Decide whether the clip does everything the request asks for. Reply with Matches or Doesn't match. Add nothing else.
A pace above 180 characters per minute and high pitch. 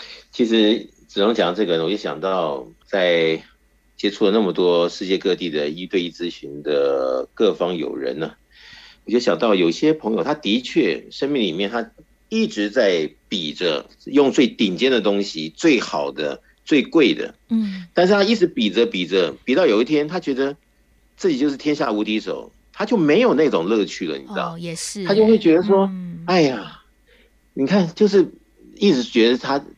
Doesn't match